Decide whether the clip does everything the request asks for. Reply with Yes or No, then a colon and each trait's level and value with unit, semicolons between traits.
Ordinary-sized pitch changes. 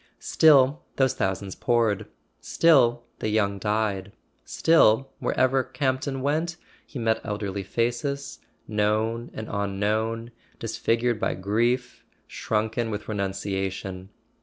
Yes: average, 3.9 semitones